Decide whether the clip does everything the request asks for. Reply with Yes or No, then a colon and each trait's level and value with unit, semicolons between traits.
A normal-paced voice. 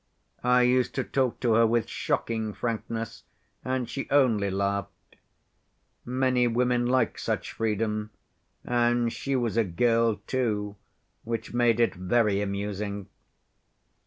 No: slow, 125 wpm